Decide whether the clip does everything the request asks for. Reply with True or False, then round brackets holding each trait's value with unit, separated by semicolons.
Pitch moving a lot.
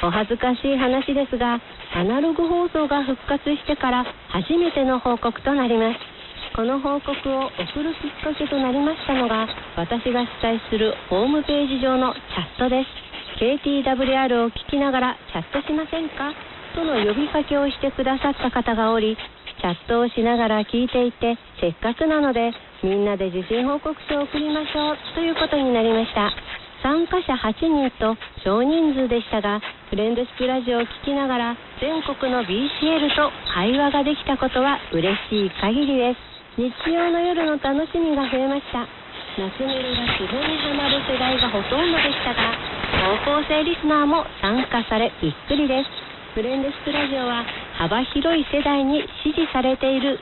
False (3.7 semitones)